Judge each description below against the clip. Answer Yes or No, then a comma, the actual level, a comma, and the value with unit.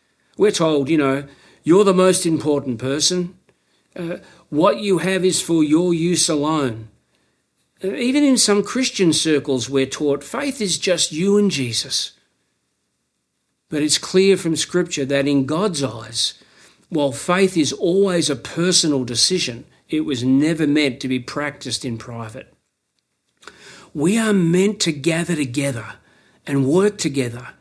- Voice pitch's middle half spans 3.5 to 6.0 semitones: Yes, average, 5.1 semitones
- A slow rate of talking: No, average, 145 wpm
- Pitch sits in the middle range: Yes, medium, 155 Hz